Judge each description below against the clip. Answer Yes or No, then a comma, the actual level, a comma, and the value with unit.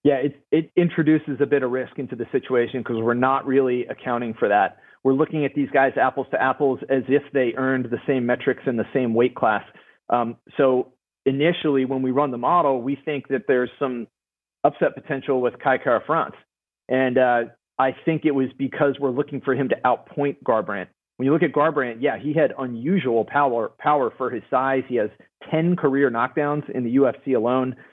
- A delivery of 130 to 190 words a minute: No, average, 200 wpm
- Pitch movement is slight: Yes, narrow, 2.2 semitones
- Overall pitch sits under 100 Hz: No, low, 135 Hz